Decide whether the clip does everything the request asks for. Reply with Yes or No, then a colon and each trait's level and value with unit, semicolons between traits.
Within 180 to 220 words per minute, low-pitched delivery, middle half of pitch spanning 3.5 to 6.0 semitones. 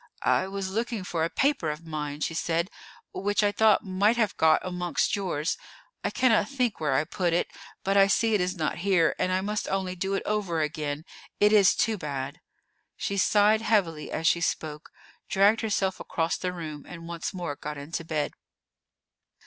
No: average, 190 wpm; medium, 185 Hz; average, 4.2 semitones